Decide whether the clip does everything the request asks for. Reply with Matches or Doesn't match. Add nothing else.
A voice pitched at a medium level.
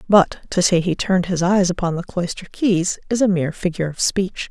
Matches